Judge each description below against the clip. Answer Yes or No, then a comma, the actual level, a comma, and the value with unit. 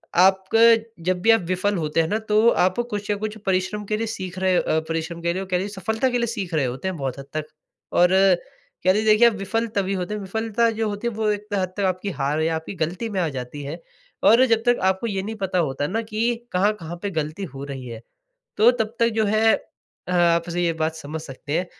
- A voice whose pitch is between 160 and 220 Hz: Yes, high, 190 Hz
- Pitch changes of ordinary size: Yes, average, 4.4 semitones